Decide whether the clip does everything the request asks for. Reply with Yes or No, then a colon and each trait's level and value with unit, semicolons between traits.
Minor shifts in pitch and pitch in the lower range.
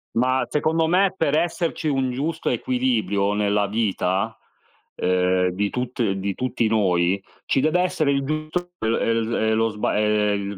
No: wide, 6.2 semitones; low, 115 Hz